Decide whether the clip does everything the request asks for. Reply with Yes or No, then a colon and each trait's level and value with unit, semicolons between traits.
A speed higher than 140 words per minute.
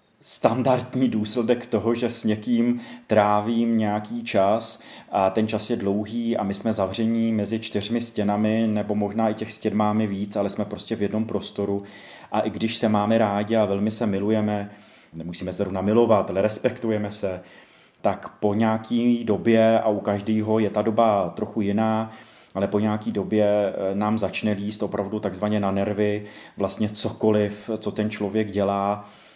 Yes: average, 165 wpm